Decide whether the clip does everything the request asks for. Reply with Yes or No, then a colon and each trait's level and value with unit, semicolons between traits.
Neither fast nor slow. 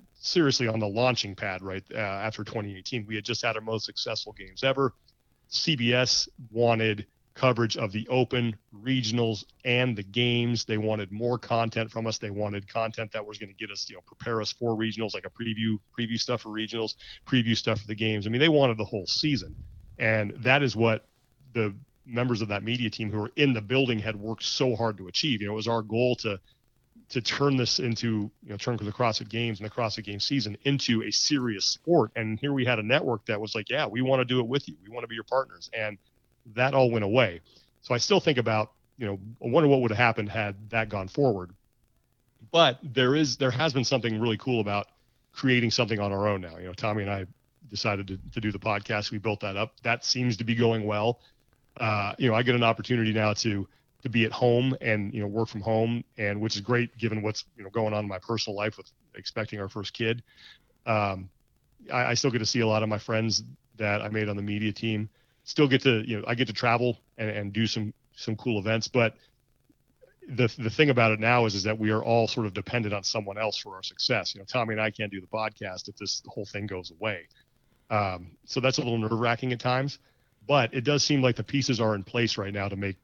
No: fast, 240 wpm